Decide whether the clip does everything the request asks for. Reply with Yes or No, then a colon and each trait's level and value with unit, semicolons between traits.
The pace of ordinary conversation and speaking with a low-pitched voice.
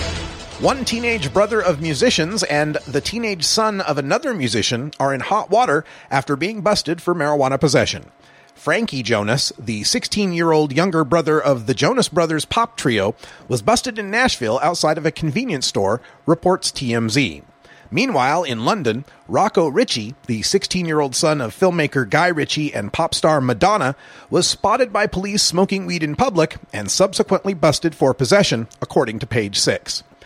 No: average, 155 wpm; medium, 155 Hz